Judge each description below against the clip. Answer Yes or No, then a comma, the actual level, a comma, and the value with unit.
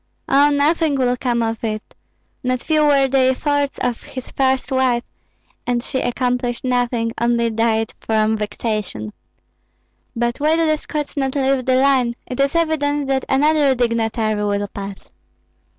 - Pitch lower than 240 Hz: No, very high, 255 Hz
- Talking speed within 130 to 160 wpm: Yes, average, 150 wpm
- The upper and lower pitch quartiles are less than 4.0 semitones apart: Yes, average, 3.2 semitones